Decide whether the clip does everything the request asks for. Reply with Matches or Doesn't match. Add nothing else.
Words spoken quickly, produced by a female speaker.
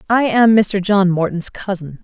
Doesn't match